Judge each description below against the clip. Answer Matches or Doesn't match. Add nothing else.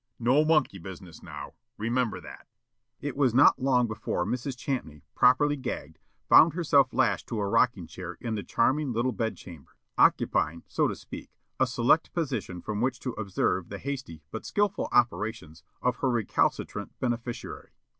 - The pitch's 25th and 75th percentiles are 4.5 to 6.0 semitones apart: Matches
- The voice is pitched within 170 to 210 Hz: Doesn't match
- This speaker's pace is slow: Doesn't match